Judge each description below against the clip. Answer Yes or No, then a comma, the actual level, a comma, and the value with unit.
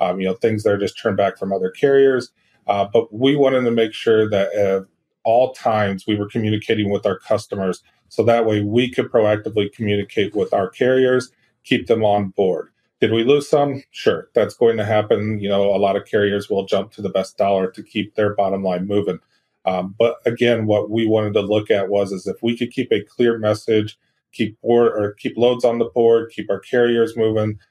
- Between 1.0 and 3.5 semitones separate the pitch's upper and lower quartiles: Yes, narrow, 2.6 semitones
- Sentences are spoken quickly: Yes, fast, 215 wpm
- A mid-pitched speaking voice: No, low, 110 Hz